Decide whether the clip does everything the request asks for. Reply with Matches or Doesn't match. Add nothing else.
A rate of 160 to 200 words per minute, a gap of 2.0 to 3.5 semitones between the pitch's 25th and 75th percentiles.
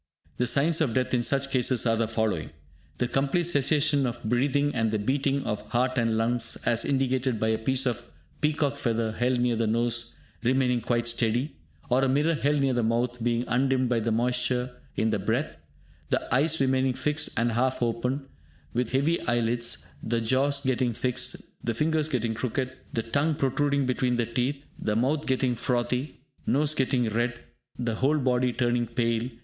Matches